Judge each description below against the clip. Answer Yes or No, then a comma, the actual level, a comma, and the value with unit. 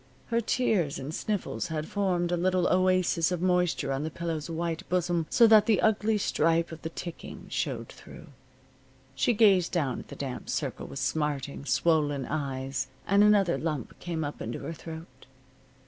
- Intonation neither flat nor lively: Yes, average, 3.7 semitones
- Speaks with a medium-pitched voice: Yes, medium, 165 Hz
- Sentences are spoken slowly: No, average, 170 wpm